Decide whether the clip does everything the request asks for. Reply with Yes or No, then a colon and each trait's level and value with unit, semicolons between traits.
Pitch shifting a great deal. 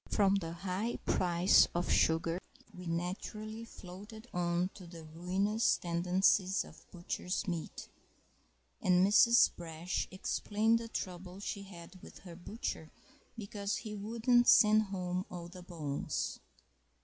No: average, 3.1 semitones